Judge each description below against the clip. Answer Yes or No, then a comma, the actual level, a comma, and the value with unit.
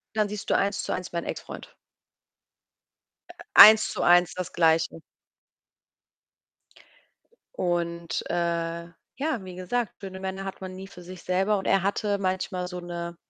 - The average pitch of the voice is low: No, medium, 185 Hz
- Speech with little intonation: Yes, narrow, 2.1 semitones